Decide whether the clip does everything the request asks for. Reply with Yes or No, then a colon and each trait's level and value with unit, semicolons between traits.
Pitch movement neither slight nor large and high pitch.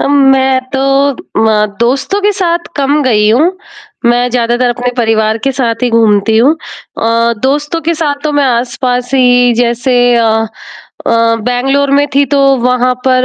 Yes: average, 3.0 semitones; very high, 250 Hz